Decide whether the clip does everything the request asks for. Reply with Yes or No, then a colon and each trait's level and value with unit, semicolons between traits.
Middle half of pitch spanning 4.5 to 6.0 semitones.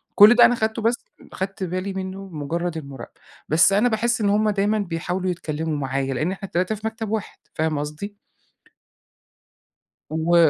Yes: average, 5.0 semitones